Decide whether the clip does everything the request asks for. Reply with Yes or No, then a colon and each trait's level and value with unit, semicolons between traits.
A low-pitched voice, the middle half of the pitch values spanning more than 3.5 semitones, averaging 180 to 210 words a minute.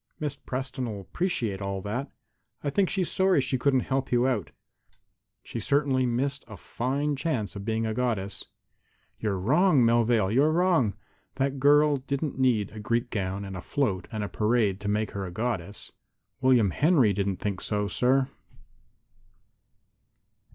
No: low, 120 Hz; average, 5.2 semitones; average, 160 wpm